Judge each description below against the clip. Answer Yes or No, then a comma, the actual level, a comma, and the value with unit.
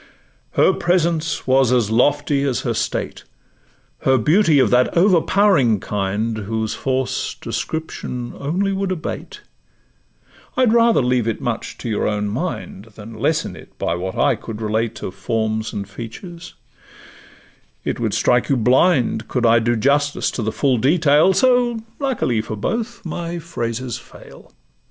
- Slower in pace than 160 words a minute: Yes, average, 145 wpm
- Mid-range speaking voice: No, low, 130 Hz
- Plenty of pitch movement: Yes, wide, 7.1 semitones